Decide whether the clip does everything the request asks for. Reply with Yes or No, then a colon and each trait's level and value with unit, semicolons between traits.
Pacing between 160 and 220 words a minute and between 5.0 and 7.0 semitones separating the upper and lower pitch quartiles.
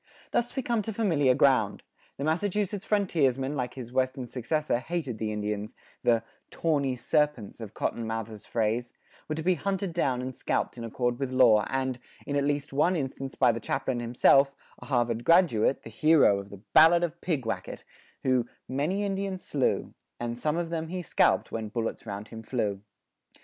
Yes: average, 180 wpm; wide, 5.6 semitones